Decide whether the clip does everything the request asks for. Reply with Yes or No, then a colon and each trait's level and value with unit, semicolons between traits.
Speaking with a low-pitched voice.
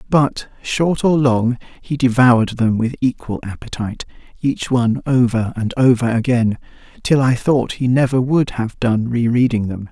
Yes: low, 125 Hz